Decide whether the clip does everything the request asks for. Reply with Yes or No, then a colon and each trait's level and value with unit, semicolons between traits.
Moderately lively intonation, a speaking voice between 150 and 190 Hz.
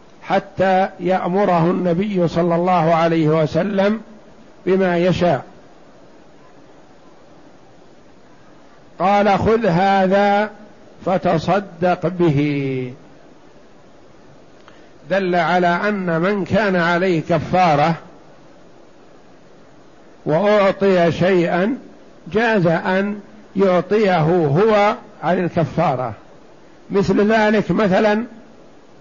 Yes: average, 3.1 semitones; medium, 185 Hz